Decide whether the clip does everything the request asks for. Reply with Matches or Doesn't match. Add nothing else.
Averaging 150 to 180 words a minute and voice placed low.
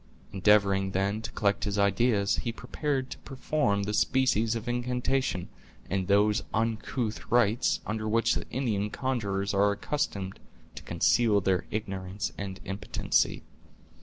Doesn't match